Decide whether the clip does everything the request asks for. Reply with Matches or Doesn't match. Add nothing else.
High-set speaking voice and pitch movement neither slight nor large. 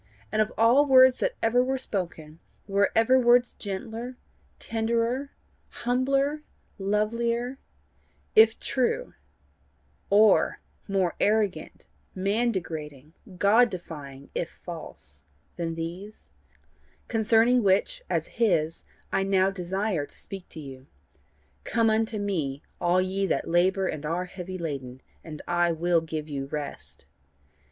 Doesn't match